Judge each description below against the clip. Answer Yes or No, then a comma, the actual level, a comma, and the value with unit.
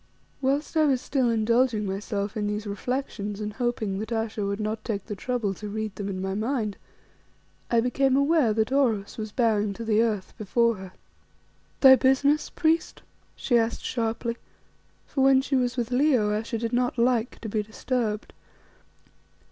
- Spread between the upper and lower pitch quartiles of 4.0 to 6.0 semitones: No, average, 3.3 semitones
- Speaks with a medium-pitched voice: No, high, 225 Hz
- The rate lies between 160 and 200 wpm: Yes, average, 170 wpm